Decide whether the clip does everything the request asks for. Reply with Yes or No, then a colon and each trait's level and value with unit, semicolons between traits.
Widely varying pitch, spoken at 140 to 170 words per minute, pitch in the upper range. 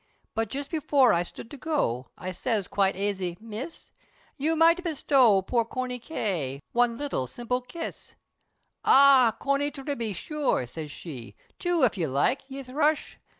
Yes: wide, 6.8 semitones; average, 150 wpm; high, 245 Hz